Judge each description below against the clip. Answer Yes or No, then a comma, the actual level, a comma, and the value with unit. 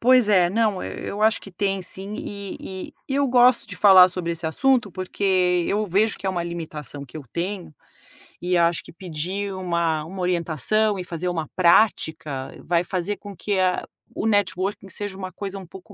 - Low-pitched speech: No, medium, 185 Hz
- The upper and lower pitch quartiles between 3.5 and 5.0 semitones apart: No, average, 3.0 semitones